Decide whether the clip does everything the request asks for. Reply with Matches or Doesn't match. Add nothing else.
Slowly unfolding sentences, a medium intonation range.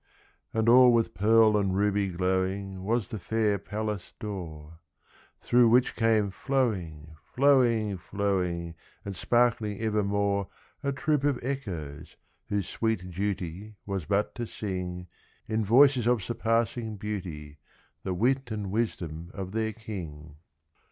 Matches